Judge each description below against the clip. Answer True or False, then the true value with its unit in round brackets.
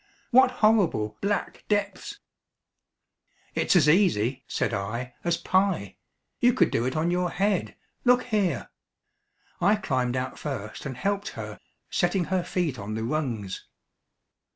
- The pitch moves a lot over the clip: True (8.1 semitones)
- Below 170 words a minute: True (140 wpm)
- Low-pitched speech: False (170 Hz)